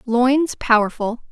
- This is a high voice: Yes, high, 240 Hz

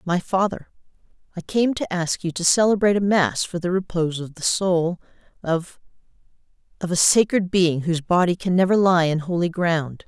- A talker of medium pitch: Yes, medium, 175 Hz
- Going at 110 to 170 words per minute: Yes, average, 165 wpm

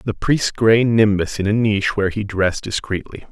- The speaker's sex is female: No, male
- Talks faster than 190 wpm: Yes, average, 200 wpm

